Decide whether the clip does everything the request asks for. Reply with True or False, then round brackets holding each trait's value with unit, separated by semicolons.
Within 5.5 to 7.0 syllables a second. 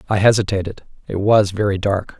True (5.7 syllables/s)